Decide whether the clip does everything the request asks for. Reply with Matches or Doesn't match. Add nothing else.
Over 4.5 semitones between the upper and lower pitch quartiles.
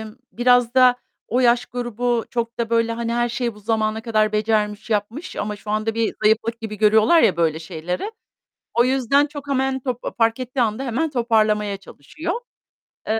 Doesn't match